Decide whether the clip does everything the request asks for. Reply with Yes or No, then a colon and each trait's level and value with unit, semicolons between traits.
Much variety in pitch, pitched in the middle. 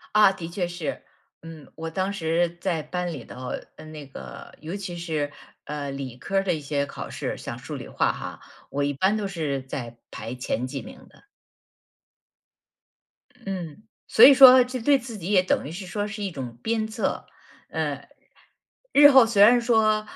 Yes: wide, 6.6 semitones; medium, 175 Hz